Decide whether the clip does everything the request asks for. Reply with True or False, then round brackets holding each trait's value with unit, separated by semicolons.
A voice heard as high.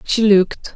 True (205 Hz)